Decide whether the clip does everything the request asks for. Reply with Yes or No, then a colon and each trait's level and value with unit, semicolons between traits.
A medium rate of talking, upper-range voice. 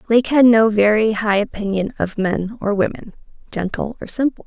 Yes: average, 175 wpm; high, 215 Hz